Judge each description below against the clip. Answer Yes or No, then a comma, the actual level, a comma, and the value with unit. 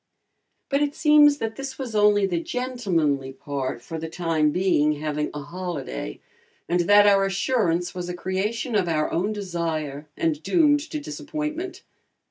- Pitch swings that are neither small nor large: No, wide, 7.9 semitones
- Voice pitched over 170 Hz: Yes, medium, 185 Hz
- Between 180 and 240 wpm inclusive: No, average, 155 wpm